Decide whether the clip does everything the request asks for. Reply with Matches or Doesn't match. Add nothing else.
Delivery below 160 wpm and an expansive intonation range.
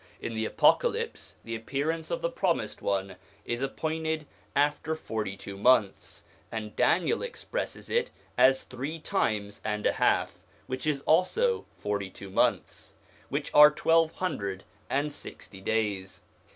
Matches